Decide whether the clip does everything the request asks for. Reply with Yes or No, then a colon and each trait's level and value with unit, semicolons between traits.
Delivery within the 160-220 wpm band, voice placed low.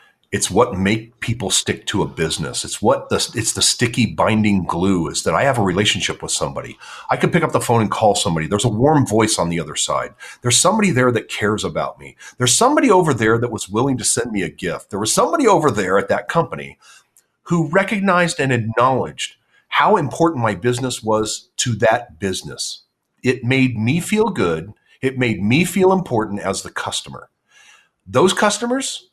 Yes: average, 195 wpm; low, 120 Hz